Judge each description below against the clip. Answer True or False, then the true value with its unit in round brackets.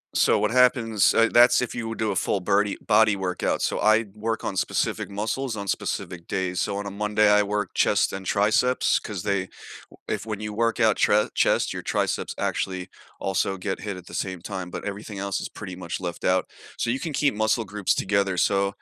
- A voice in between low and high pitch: False (105 Hz)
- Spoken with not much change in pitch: True (2.3 semitones)